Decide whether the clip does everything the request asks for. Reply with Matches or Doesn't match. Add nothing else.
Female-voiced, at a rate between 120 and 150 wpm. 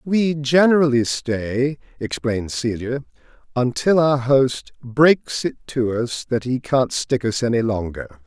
Doesn't match